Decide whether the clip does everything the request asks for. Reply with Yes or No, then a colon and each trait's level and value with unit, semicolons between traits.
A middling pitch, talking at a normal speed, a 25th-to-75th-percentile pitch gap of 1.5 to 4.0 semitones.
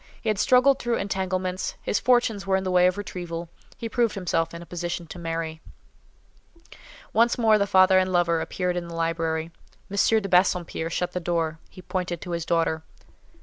Yes: medium, 180 Hz; average, 190 wpm; average, 2.8 semitones